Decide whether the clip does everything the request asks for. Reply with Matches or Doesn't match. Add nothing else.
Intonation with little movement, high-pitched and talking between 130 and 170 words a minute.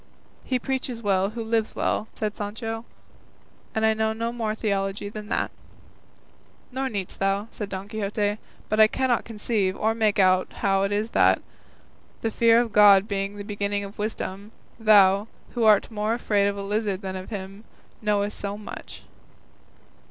Matches